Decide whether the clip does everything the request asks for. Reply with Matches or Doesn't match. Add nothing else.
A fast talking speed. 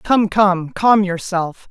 Doesn't match